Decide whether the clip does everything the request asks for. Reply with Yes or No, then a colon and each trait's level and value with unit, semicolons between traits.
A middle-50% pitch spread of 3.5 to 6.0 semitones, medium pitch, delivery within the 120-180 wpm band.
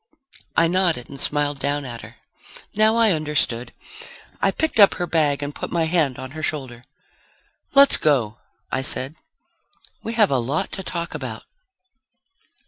Yes: average, 4.9 semitones; medium, 150 Hz; average, 155 wpm